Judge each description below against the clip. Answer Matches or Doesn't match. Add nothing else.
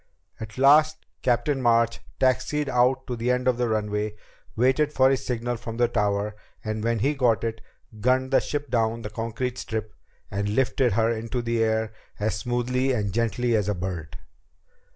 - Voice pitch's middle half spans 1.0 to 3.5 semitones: Matches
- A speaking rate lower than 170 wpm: Doesn't match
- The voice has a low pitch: Matches